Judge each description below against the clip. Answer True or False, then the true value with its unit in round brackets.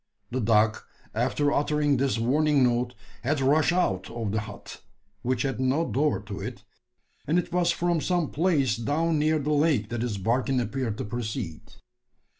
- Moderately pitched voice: False (130 Hz)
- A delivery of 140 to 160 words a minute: False (170 wpm)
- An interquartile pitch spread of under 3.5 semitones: False (4.7 semitones)